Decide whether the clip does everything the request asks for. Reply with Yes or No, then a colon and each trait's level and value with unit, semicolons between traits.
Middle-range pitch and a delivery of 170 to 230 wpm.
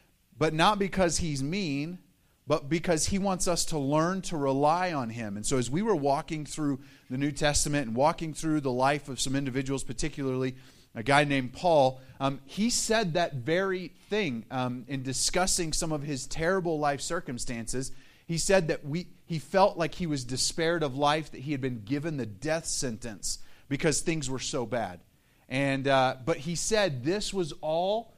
Yes: medium, 145 Hz; average, 185 wpm